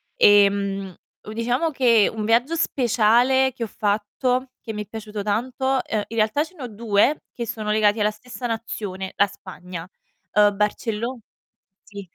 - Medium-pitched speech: No, high, 220 Hz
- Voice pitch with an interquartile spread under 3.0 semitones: No, average, 3.3 semitones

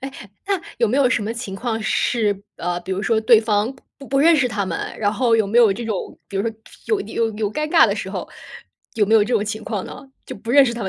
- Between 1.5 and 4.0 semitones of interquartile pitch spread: Yes, average, 3.3 semitones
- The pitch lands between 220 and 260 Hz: Yes, high, 225 Hz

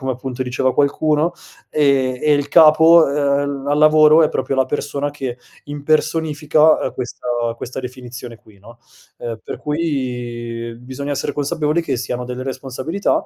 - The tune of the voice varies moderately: Yes, average, 3.3 semitones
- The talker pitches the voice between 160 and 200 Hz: No, medium, 140 Hz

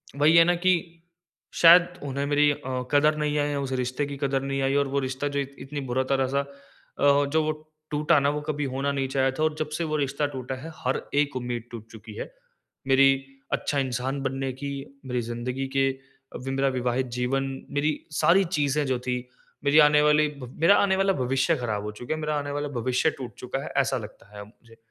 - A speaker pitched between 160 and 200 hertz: No, medium, 140 Hz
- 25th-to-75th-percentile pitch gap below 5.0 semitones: Yes, narrow, 2.4 semitones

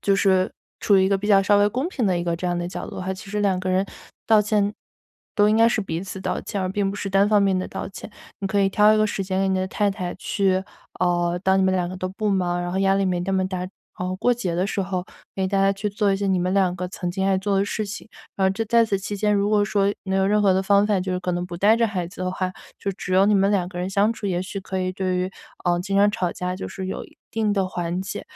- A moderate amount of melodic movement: No, narrow, 1.7 semitones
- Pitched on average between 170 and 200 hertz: Yes, high, 195 Hz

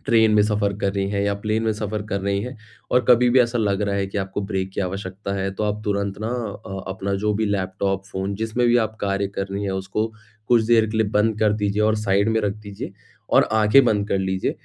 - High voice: No, low, 105 Hz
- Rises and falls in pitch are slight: Yes, narrow, 2.0 semitones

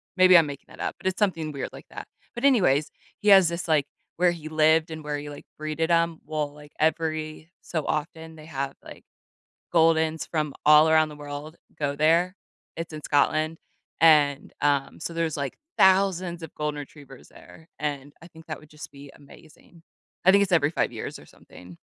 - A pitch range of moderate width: No, narrow, 2.1 semitones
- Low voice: No, medium, 155 Hz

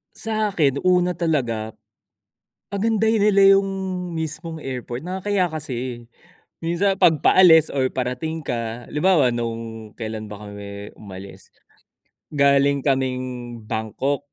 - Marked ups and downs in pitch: Yes, wide, 7.5 semitones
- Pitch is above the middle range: No, medium, 140 Hz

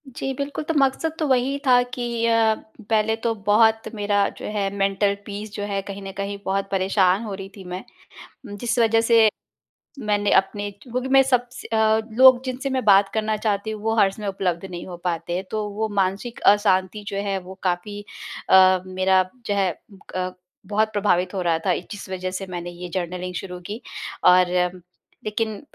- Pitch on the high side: Yes, high, 205 Hz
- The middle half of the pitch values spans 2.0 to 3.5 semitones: Yes, average, 3.0 semitones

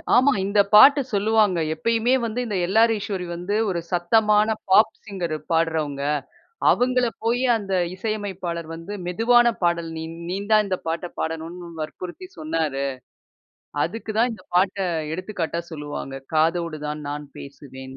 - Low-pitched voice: No, medium, 185 Hz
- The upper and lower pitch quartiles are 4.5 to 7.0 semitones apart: Yes, average, 4.9 semitones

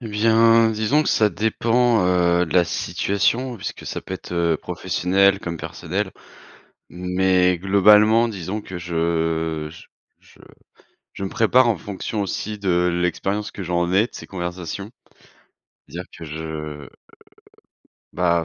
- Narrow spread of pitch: No, average, 3.7 semitones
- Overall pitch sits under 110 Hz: Yes, very low, 95 Hz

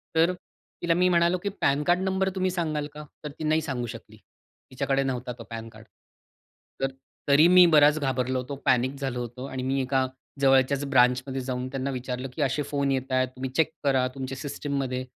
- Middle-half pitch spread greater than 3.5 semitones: No, average, 2.8 semitones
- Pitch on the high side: No, low, 135 Hz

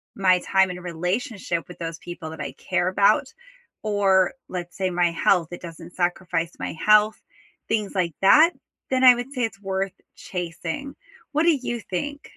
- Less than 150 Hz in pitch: No, medium, 185 Hz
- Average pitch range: Yes, average, 3.4 semitones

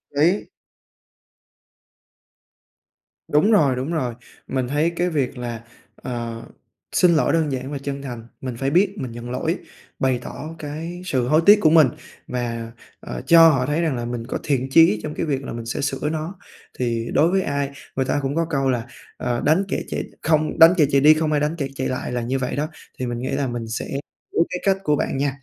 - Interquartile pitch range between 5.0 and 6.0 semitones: No, average, 4.2 semitones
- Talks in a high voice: No, medium, 140 Hz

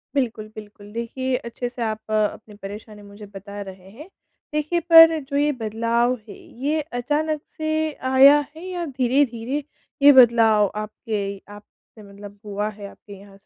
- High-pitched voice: Yes, high, 230 Hz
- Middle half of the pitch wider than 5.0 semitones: Yes, wide, 5.5 semitones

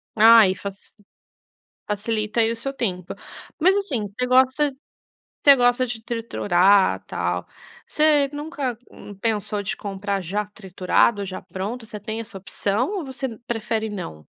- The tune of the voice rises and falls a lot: No, average, 4.1 semitones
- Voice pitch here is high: Yes, high, 220 Hz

